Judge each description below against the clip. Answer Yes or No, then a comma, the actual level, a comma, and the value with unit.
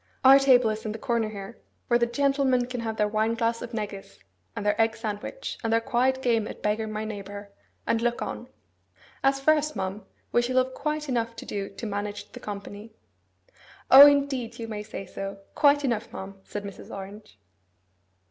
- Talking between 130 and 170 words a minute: No, average, 190 wpm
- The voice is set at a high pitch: Yes, high, 225 Hz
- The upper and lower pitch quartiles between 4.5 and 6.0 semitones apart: No, average, 3.6 semitones